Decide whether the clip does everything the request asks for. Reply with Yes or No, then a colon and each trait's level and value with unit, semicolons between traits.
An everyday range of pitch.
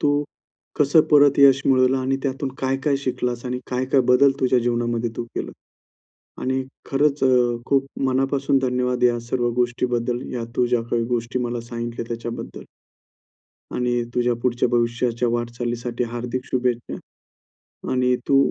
No: narrow, 1.8 semitones